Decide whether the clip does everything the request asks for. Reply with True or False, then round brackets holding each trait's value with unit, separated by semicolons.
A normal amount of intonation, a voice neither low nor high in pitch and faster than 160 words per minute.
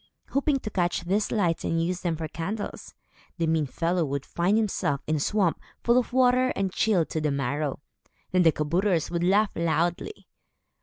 True (4.4 semitones; 175 Hz; 185 wpm)